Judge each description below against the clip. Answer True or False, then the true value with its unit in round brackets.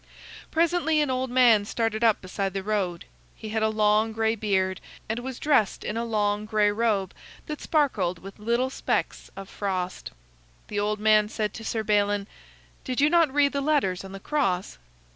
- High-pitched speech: True (215 Hz)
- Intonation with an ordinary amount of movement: True (3.9 semitones)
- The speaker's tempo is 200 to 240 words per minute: False (180 wpm)